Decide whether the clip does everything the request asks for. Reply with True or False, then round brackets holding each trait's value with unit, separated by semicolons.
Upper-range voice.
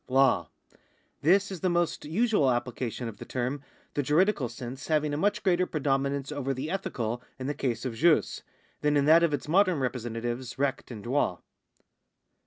False (140 Hz)